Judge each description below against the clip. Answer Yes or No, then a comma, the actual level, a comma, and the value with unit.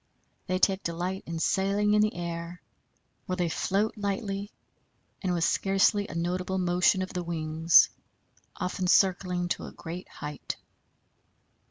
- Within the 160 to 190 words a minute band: No, average, 140 wpm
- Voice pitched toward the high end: No, medium, 180 Hz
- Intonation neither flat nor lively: No, narrow, 2.2 semitones